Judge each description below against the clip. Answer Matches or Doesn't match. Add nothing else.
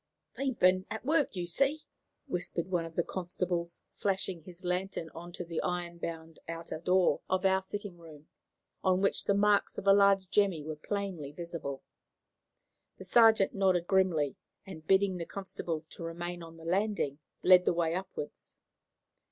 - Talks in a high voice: Doesn't match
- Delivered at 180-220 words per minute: Doesn't match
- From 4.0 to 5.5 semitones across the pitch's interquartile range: Doesn't match